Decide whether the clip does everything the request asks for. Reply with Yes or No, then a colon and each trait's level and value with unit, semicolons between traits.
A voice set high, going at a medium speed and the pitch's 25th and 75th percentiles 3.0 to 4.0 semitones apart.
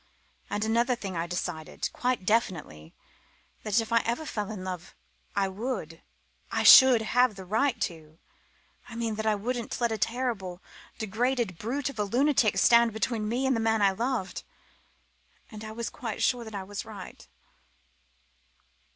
Yes: high, 220 Hz; average, 165 wpm; average, 3.7 semitones